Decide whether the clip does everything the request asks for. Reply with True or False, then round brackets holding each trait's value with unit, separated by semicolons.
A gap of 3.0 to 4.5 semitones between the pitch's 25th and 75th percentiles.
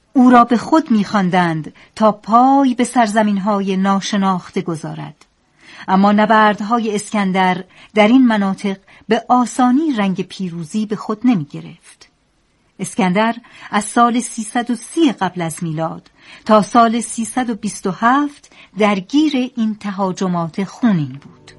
True (3.9 semitones)